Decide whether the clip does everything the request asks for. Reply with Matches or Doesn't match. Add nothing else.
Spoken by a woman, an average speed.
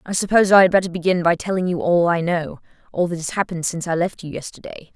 Doesn't match